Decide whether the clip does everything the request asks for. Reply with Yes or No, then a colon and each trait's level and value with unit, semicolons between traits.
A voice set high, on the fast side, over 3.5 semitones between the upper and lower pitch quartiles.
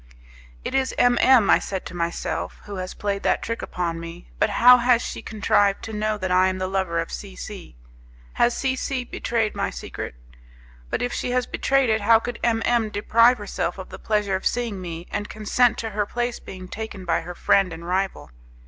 Yes: high, 210 Hz; fast, 210 wpm; average, 4.1 semitones